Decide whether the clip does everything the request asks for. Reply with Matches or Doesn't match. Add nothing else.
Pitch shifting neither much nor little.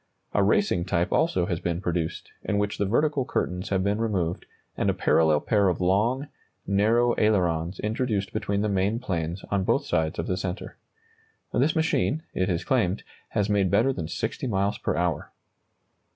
Matches